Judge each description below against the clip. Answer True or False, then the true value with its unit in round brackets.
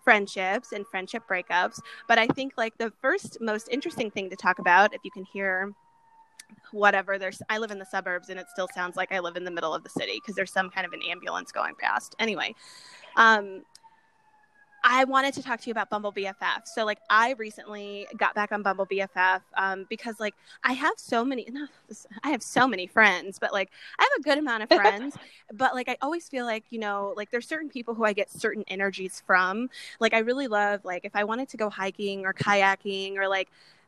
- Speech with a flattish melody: False (4.3 semitones)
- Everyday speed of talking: False (220 wpm)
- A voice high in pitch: True (210 Hz)